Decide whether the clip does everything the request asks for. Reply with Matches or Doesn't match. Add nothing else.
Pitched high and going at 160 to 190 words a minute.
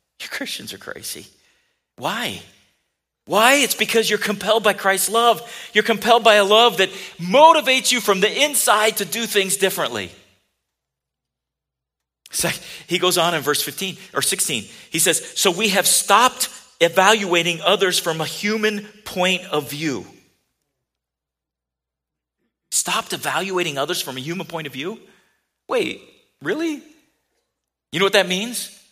Doesn't match